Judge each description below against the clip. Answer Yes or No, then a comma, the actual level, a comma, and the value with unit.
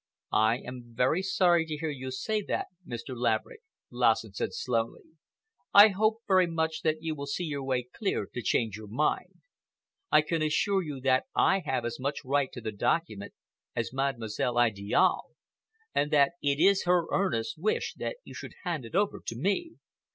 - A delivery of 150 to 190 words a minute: Yes, average, 180 wpm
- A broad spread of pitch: Yes, wide, 6.5 semitones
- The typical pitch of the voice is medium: Yes, medium, 145 Hz